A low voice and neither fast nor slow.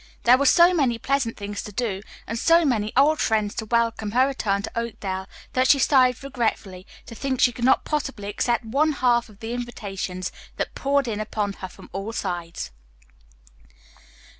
No: high, 230 Hz; average, 180 wpm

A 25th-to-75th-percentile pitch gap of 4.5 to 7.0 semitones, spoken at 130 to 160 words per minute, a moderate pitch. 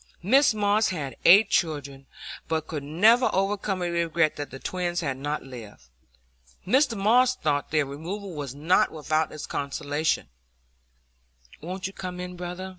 Yes: average, 4.9 semitones; average, 150 wpm; medium, 170 Hz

